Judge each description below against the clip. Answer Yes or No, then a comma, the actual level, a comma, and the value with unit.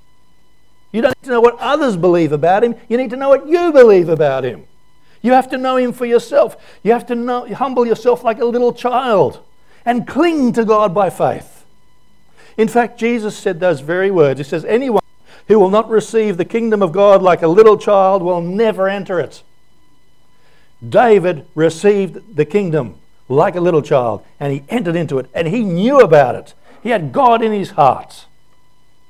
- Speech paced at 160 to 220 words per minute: Yes, average, 190 wpm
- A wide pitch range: Yes, wide, 5.8 semitones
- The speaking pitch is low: No, high, 210 Hz